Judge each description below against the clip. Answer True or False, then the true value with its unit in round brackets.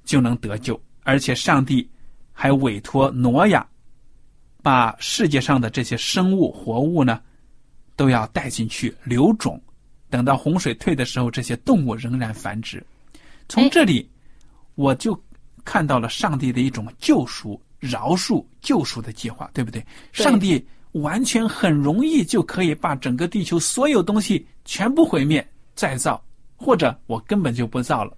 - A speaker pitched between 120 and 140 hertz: True (135 Hz)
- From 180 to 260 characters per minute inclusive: True (230 characters per minute)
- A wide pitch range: True (6.1 semitones)